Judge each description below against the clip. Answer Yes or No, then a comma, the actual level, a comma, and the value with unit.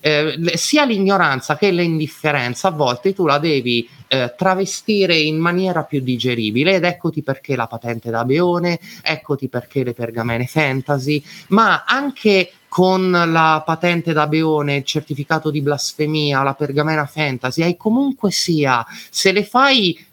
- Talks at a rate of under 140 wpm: No, average, 145 wpm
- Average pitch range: Yes, average, 4.6 semitones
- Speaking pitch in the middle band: Yes, medium, 155 Hz